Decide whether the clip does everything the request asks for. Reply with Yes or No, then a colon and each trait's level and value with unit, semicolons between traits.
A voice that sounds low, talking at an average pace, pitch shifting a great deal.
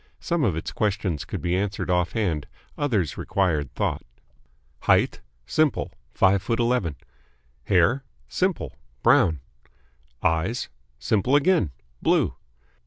No: very low, 95 Hz; slow, 110 wpm; wide, 6.1 semitones